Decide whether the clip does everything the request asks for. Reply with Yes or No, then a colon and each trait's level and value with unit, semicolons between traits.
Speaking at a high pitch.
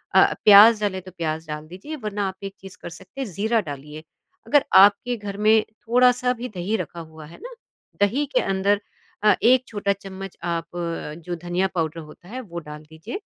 Yes: high, 195 Hz